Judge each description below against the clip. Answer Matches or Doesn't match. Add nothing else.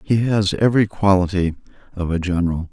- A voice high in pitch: Doesn't match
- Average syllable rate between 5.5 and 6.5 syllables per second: Matches